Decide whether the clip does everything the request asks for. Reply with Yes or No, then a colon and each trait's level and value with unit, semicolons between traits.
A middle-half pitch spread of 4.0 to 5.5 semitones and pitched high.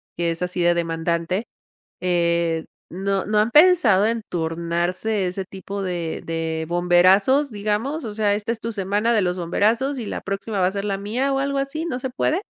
Yes: average, 4.6 semitones; high, 195 Hz